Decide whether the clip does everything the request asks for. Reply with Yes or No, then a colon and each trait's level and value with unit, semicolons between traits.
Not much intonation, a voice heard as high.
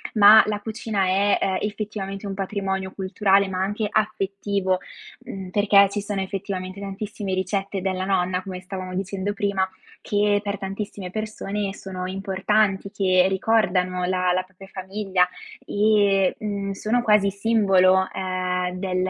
Yes: narrow, 1.6 semitones; high, 195 Hz